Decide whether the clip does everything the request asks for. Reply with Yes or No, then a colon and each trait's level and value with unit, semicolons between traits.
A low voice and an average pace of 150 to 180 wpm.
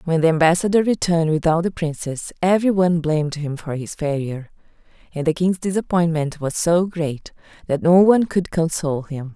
No: medium, 165 Hz; average, 175 wpm